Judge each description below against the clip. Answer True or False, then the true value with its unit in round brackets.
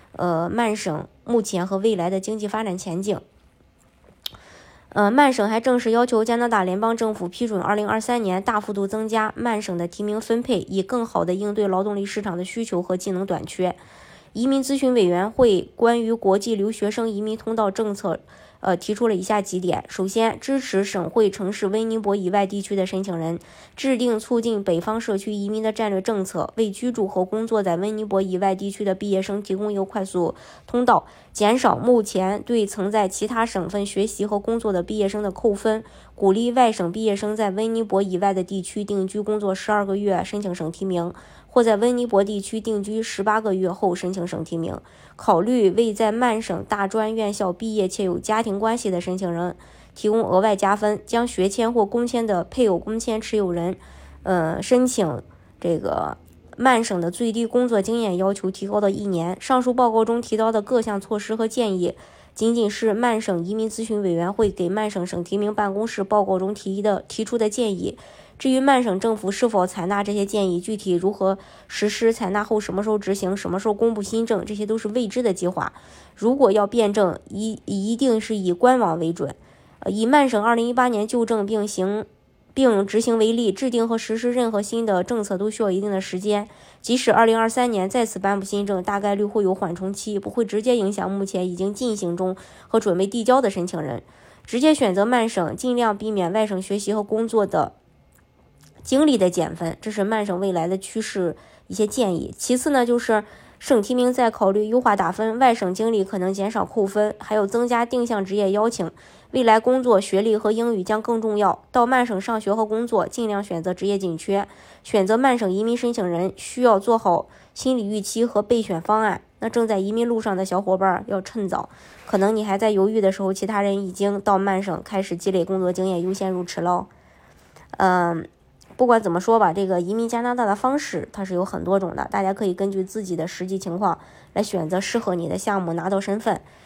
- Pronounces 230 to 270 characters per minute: False (305 characters per minute)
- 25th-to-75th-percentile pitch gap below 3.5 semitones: True (2.8 semitones)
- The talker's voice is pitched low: False (205 Hz)